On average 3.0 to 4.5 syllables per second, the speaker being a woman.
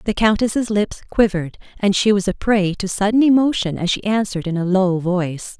No: 5.5 syllables/s; female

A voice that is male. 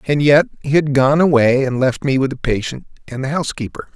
Yes: male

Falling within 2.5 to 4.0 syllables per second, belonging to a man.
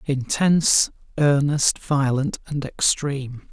Yes: 3.6 syllables/s; male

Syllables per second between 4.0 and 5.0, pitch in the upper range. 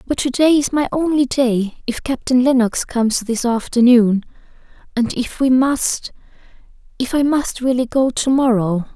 Yes: 4.5 syllables/s; very high, 250 Hz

